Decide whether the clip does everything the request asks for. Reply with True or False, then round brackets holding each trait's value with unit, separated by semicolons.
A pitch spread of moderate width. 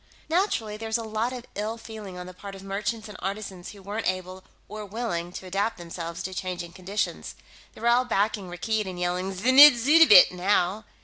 True (3.3 semitones)